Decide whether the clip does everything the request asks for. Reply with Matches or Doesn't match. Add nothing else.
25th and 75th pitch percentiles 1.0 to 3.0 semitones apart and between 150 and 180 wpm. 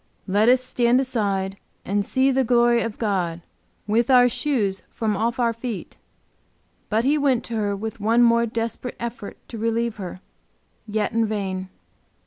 Matches